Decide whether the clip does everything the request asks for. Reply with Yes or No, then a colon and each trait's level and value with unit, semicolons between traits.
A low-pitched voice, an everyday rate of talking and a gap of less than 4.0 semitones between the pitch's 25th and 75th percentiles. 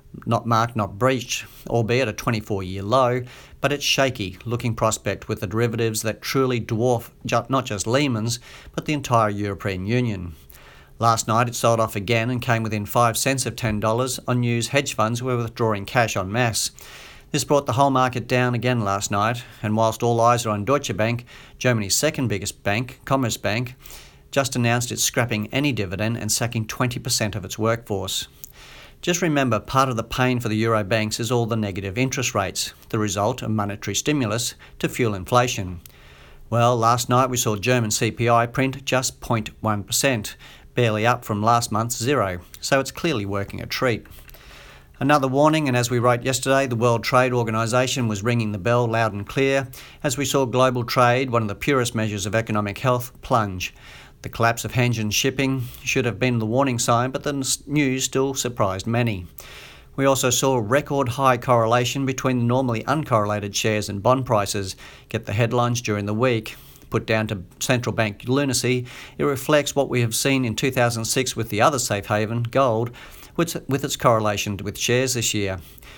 Yes: low, 120 Hz; average, 175 wpm; average, 3.2 semitones